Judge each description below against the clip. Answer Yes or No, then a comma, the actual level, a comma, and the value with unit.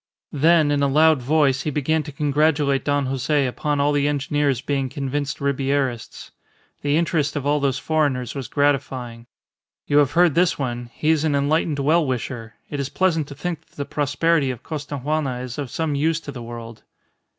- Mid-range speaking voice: Yes, medium, 145 Hz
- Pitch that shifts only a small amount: Yes, narrow, 2.2 semitones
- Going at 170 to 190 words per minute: Yes, average, 185 wpm